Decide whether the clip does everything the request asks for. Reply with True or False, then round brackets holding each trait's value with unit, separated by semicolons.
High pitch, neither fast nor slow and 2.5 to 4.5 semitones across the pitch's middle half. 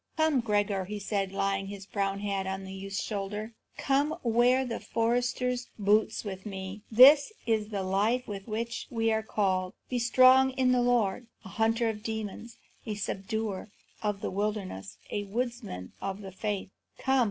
True (210 Hz; 170 wpm; 3.5 semitones)